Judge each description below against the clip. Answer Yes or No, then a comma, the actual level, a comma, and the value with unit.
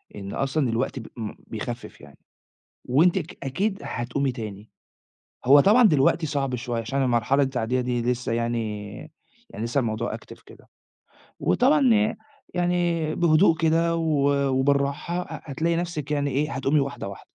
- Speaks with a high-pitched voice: No, medium, 140 Hz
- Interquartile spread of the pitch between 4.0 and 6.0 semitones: Yes, wide, 5.4 semitones